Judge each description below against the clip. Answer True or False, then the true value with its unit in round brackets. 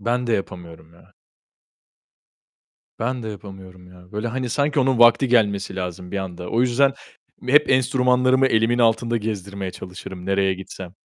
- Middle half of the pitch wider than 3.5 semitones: True (5.0 semitones)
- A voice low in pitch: True (110 Hz)